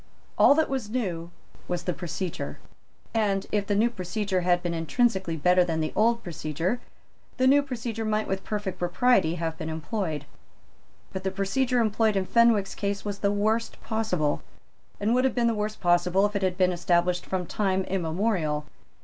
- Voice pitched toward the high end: Yes, high, 195 Hz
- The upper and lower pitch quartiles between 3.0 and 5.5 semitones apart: Yes, average, 4.0 semitones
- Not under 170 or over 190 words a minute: Yes, average, 175 wpm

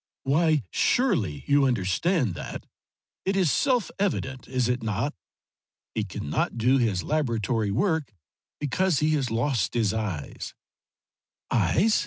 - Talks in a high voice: No, low, 130 Hz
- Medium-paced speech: No, slow, 120 wpm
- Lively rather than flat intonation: Yes, wide, 5.9 semitones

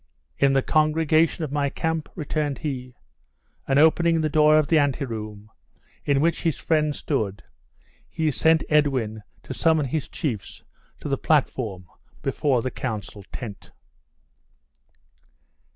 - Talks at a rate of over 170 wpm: No, slow, 135 wpm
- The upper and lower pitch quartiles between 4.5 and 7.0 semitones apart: No, average, 3.6 semitones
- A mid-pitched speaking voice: Yes, medium, 145 Hz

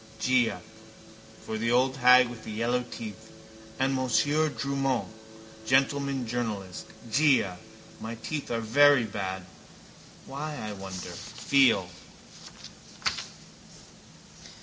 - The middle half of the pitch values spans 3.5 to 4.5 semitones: Yes, average, 3.9 semitones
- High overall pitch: No, low, 125 Hz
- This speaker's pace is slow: Yes, slow, 95 wpm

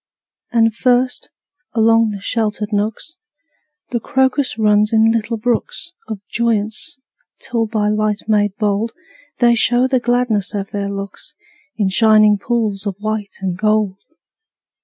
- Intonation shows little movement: Yes, narrow, 2.2 semitones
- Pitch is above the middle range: Yes, high, 215 Hz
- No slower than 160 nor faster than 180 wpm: No, slow, 135 wpm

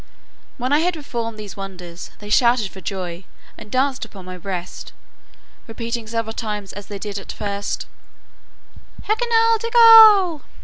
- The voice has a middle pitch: No, high, 225 Hz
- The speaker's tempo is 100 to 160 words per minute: Yes, average, 140 wpm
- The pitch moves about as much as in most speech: No, wide, 7.2 semitones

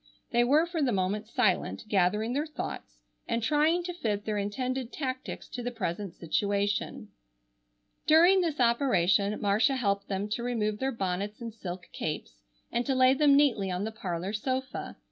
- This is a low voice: No, high, 225 Hz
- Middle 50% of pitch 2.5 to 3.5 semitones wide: No, average, 4.8 semitones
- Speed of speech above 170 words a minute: No, average, 165 wpm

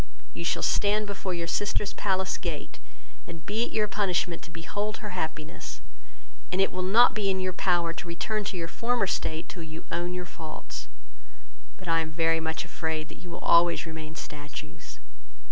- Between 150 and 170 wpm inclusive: No, average, 185 wpm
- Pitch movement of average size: Yes, average, 3.3 semitones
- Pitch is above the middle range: No, medium, 175 Hz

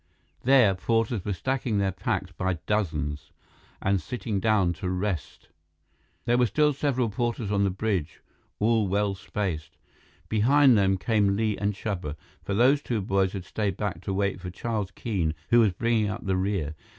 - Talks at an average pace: Yes, average, 170 wpm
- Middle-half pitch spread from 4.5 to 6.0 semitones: No, average, 3.3 semitones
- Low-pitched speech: Yes, low, 100 Hz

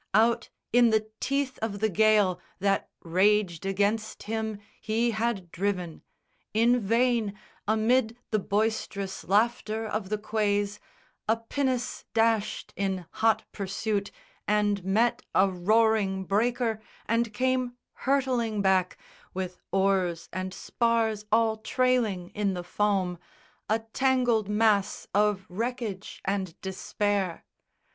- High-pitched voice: Yes, high, 215 Hz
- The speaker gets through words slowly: Yes, slow, 115 wpm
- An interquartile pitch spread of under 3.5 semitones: Yes, average, 2.7 semitones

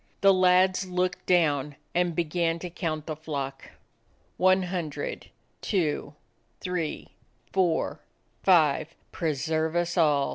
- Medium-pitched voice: Yes, medium, 170 Hz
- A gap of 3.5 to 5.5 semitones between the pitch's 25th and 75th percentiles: No, average, 2.8 semitones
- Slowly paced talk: Yes, slow, 115 wpm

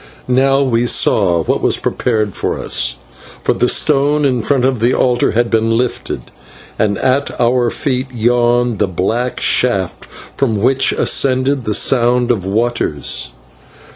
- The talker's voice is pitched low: Yes, low, 120 Hz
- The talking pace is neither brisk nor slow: Yes, average, 145 wpm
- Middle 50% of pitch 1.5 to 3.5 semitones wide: Yes, average, 2.8 semitones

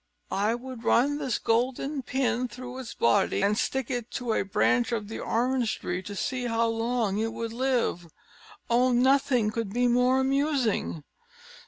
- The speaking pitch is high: Yes, high, 240 Hz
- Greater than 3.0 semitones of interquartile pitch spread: No, narrow, 2.4 semitones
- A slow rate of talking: No, average, 165 wpm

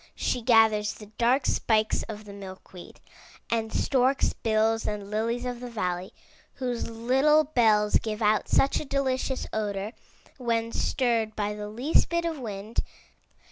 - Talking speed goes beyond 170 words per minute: No, average, 150 wpm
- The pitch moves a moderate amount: Yes, average, 3.0 semitones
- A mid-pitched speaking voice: No, high, 225 Hz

